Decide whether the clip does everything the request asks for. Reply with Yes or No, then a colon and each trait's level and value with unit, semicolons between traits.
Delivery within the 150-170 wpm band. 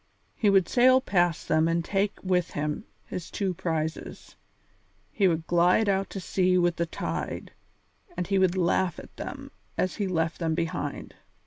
Yes: average, 165 wpm